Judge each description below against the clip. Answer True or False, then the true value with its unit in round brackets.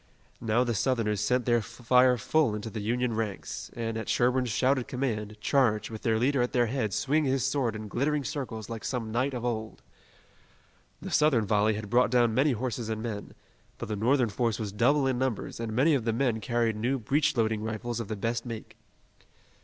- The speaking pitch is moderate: False (120 Hz)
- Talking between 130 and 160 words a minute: False (200 wpm)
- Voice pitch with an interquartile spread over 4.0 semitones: False (2.8 semitones)